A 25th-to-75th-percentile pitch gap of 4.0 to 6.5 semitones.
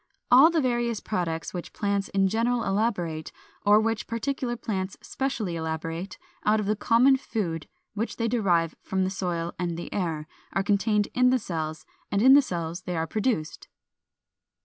Yes: average, 5.3 semitones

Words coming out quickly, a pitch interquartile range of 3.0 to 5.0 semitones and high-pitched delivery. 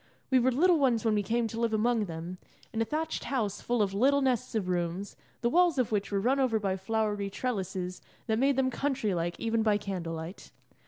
Yes: fast, 220 wpm; average, 4.6 semitones; high, 220 Hz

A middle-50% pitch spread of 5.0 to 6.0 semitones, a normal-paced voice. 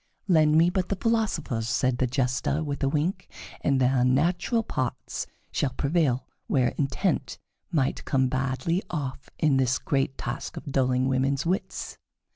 No: average, 3.9 semitones; average, 150 wpm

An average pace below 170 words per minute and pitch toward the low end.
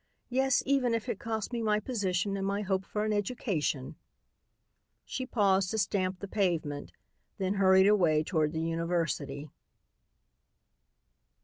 No: slow, 135 wpm; high, 195 Hz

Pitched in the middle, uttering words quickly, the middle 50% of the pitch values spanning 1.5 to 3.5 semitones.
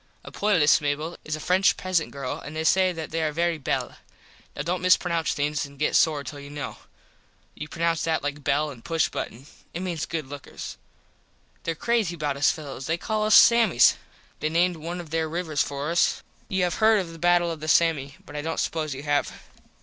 Yes: medium, 160 Hz; fast, 215 wpm; average, 2.9 semitones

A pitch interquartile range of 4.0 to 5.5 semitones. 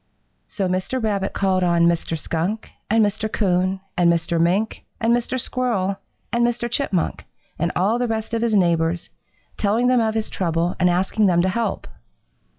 Yes: average, 4.3 semitones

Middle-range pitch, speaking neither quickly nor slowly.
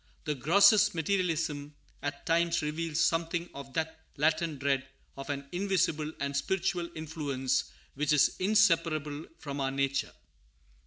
No: medium, 155 Hz; slow, 125 wpm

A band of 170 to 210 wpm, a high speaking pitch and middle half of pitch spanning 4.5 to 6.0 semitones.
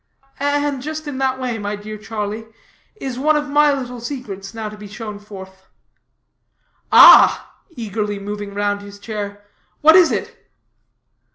No: average, 150 wpm; high, 220 Hz; average, 5.0 semitones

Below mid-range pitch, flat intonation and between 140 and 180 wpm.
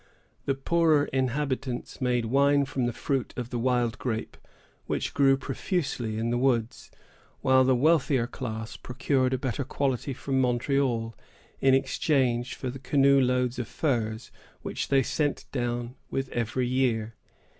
Yes: low, 130 Hz; narrow, 2.1 semitones; average, 145 wpm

